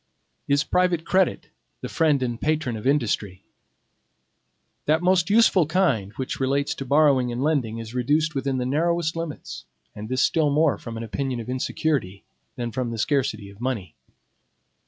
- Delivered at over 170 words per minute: No, average, 160 wpm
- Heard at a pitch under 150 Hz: Yes, low, 135 Hz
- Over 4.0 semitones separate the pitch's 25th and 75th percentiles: Yes, average, 5.0 semitones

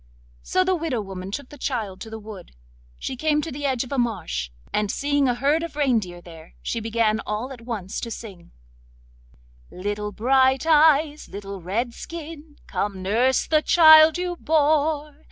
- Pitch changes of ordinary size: No, wide, 6.3 semitones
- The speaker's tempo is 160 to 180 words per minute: Yes, average, 170 wpm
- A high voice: Yes, very high, 250 Hz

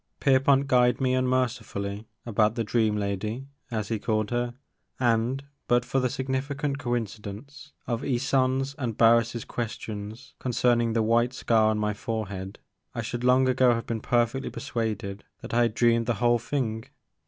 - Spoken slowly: No, average, 160 wpm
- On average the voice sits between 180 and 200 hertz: No, low, 120 Hz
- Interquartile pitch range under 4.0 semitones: Yes, average, 2.7 semitones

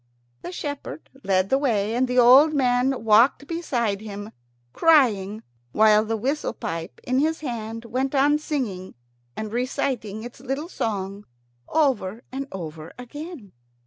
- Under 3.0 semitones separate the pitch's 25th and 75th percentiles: No, average, 4.7 semitones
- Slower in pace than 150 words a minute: Yes, average, 140 wpm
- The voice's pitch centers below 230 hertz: No, high, 245 Hz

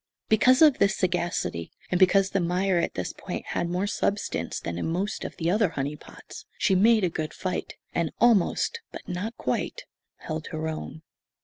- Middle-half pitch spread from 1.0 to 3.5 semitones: No, average, 3.9 semitones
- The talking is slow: No, average, 185 wpm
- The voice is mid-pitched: Yes, medium, 180 Hz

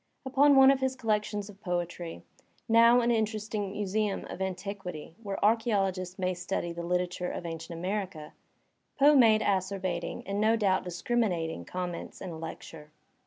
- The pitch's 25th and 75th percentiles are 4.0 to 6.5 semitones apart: No, average, 3.6 semitones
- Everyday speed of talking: Yes, average, 160 wpm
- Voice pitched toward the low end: No, high, 195 Hz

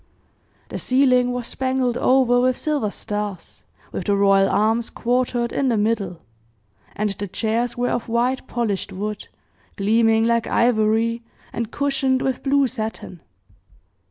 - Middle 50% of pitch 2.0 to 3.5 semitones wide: Yes, average, 3.0 semitones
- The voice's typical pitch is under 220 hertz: No, high, 235 Hz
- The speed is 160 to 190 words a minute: No, slow, 135 wpm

